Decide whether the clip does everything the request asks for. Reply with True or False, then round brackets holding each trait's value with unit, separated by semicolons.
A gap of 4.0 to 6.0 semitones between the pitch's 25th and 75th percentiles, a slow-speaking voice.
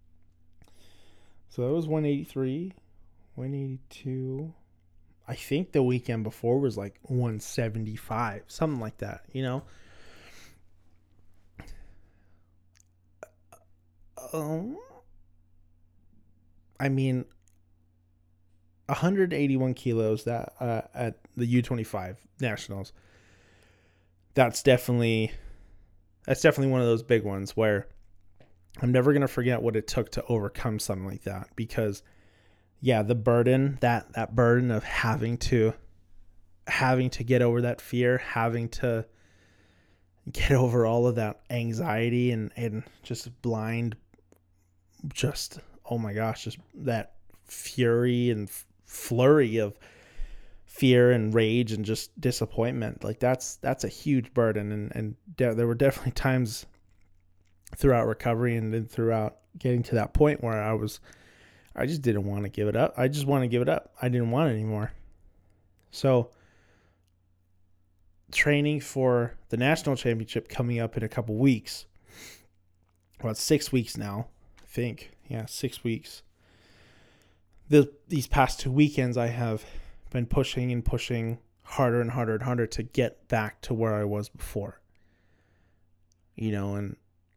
True (5.2 semitones; 130 wpm)